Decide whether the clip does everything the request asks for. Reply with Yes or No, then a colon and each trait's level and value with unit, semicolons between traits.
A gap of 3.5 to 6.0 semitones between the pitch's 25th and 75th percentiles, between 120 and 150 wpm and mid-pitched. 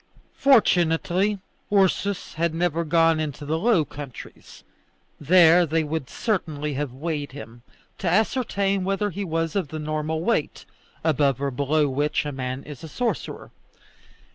Yes: average, 4.1 semitones; average, 140 wpm; medium, 160 Hz